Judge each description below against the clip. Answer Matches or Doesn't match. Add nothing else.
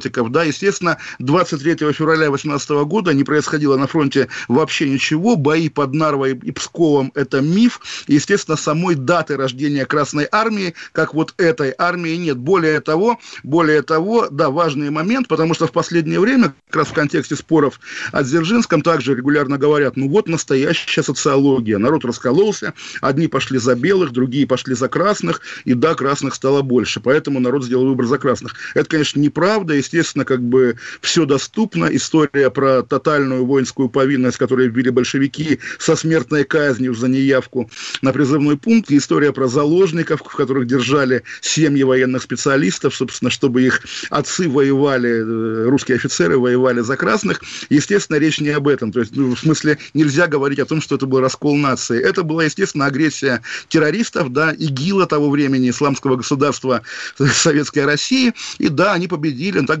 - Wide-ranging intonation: Doesn't match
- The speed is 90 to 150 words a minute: Doesn't match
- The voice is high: Doesn't match